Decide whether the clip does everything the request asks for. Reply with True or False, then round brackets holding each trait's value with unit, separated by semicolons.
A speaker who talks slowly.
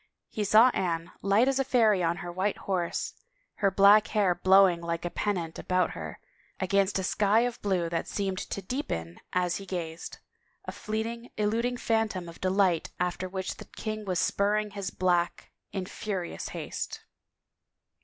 False (165 wpm)